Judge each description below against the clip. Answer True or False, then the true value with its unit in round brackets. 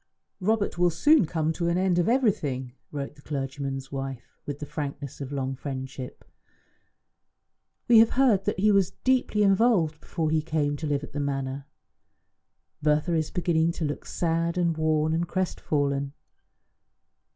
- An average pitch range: True (4.2 semitones)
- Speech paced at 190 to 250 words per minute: False (155 wpm)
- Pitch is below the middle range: False (155 Hz)